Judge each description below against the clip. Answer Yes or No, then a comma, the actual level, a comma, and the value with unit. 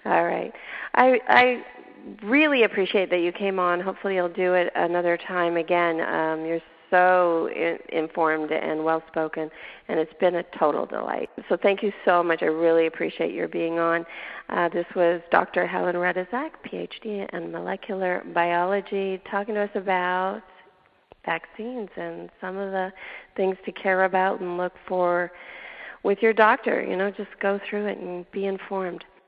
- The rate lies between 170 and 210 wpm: No, average, 160 wpm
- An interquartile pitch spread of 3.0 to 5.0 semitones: No, narrow, 2.5 semitones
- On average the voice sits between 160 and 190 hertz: Yes, medium, 185 Hz